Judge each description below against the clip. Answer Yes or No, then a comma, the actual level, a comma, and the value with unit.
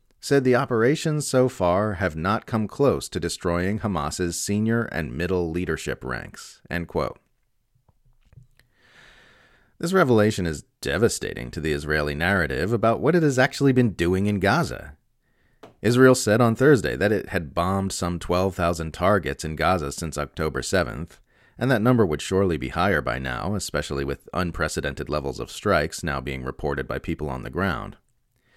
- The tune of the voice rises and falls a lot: Yes, wide, 6.7 semitones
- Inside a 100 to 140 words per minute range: No, average, 160 wpm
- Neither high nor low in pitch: No, very low, 95 Hz